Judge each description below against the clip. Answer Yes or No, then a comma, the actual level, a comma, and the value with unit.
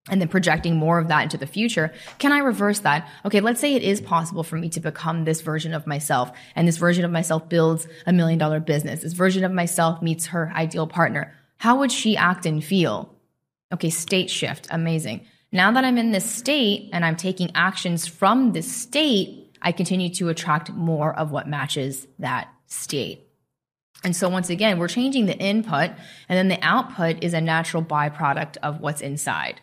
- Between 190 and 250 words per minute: Yes, average, 195 wpm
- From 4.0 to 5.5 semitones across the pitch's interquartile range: No, average, 3.2 semitones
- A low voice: No, medium, 170 Hz